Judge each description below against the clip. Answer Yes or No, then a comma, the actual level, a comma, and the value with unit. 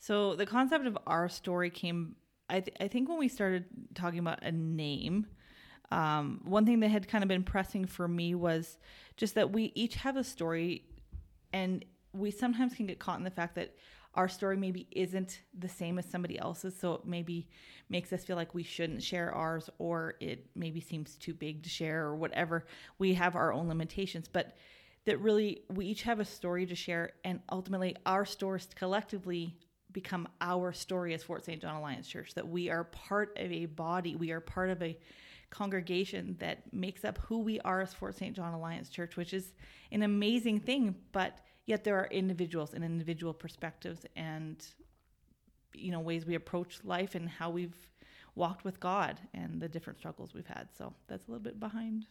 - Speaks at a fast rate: No, average, 195 wpm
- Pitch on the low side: No, medium, 180 Hz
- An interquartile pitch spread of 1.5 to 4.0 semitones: Yes, average, 2.9 semitones